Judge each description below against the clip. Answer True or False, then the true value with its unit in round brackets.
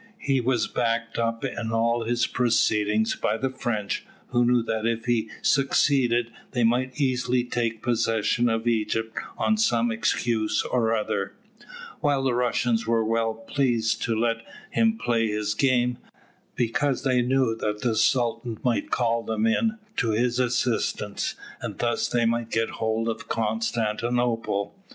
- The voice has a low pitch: True (115 Hz)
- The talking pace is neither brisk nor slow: True (150 wpm)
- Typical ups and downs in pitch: False (1.6 semitones)